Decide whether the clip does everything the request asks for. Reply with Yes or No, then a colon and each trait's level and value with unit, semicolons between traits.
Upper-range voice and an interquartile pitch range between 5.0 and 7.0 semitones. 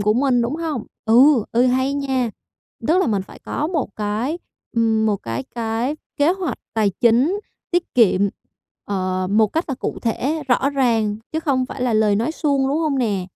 No: high, 245 Hz; average, 4.6 semitones